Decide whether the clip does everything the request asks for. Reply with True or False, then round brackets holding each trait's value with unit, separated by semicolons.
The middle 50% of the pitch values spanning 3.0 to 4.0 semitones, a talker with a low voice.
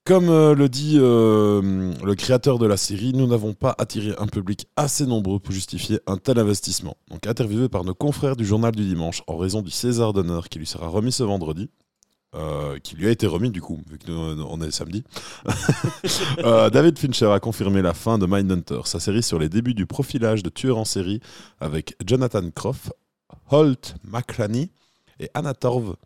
False (5.3 semitones; 105 Hz)